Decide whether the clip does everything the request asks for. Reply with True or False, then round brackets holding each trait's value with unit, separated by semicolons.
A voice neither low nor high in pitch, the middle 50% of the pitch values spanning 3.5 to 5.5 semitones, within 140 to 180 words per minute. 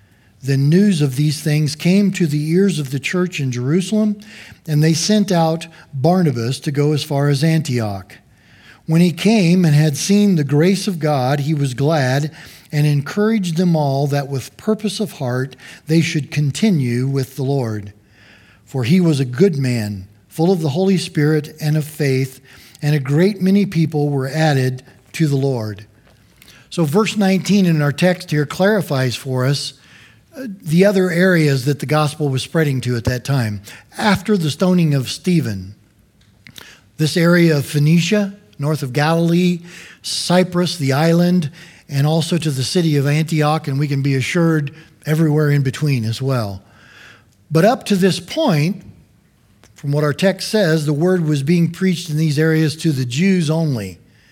True (150 Hz; 4.4 semitones; 170 wpm)